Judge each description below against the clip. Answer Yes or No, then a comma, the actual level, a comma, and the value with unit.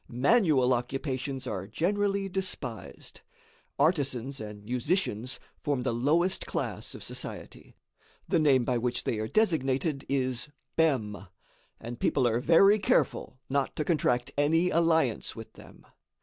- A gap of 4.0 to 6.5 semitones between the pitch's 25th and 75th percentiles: Yes, average, 5.1 semitones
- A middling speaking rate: No, slow, 130 wpm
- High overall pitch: No, low, 135 Hz